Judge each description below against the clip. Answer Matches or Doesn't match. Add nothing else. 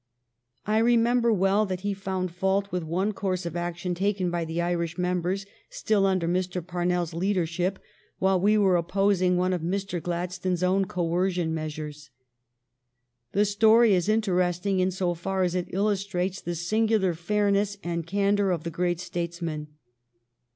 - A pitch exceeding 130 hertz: Matches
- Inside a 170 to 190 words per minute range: Doesn't match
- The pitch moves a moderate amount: Doesn't match